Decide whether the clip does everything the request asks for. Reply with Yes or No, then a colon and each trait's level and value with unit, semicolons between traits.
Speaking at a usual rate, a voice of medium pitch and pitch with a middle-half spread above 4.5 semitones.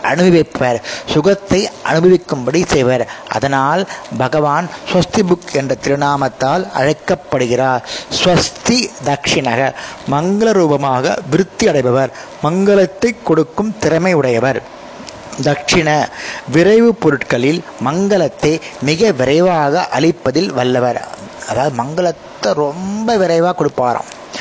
Yes: average, 85 wpm; medium, 155 Hz; average, 5.2 semitones